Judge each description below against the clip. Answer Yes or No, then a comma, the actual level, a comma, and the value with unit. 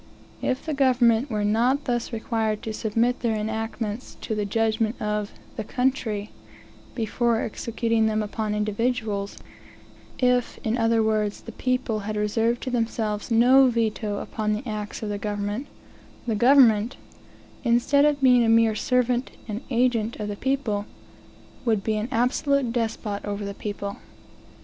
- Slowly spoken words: No, average, 150 wpm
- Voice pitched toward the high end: Yes, high, 225 Hz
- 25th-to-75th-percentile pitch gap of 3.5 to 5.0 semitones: No, narrow, 2.6 semitones